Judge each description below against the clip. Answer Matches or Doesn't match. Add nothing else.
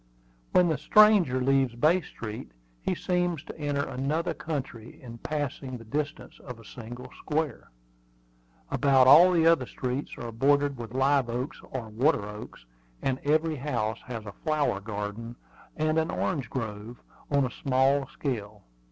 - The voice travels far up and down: Doesn't match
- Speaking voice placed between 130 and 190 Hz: Matches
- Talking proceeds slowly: Doesn't match